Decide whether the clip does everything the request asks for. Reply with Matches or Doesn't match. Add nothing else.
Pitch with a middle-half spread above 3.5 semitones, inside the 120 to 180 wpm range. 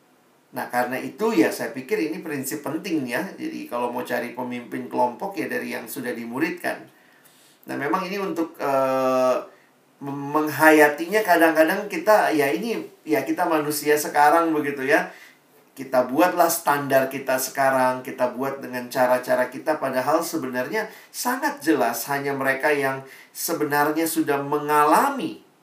Matches